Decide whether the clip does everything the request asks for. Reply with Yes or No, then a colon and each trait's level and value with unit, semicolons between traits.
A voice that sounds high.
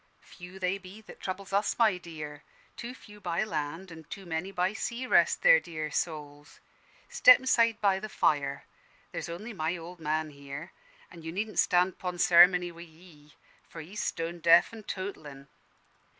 No: medium, 175 Hz